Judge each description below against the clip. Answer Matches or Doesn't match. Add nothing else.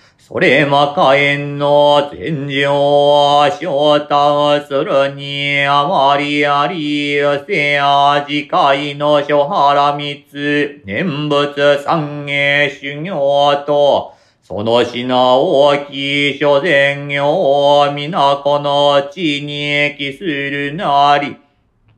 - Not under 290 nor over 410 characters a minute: Doesn't match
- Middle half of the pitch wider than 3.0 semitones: Doesn't match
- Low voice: Doesn't match